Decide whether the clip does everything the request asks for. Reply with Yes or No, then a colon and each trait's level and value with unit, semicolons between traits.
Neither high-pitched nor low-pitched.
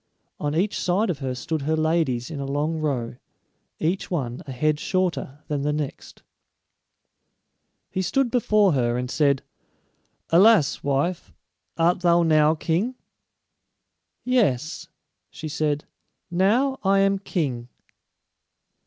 Yes: medium, 155 Hz